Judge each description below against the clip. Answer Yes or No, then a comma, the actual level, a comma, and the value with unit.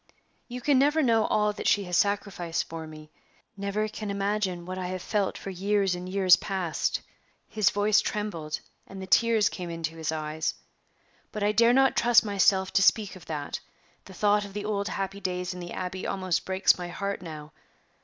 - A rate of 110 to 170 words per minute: No, average, 195 wpm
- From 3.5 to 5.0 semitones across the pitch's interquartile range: No, average, 2.8 semitones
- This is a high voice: Yes, high, 195 Hz